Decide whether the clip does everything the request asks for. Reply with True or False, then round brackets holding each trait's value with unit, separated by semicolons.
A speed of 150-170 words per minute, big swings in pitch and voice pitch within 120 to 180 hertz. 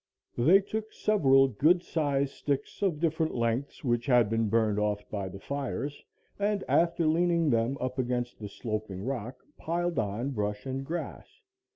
True (160 wpm; 6.3 semitones; 135 Hz)